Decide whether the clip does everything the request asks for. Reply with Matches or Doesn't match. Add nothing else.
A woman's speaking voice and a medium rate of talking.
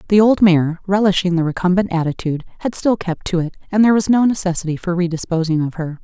Doesn't match